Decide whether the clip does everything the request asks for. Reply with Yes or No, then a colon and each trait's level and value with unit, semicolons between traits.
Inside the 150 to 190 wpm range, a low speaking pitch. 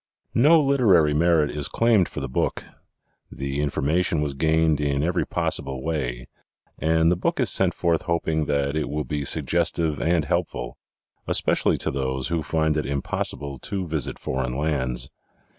Yes: average, 160 wpm; very low, 75 Hz